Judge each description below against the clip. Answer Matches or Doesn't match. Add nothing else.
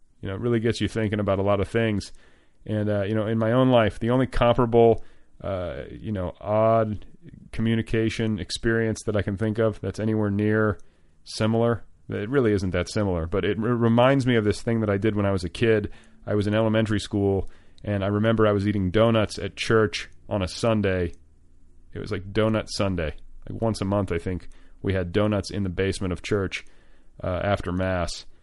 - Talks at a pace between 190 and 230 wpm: Matches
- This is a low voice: Matches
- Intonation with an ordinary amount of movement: Matches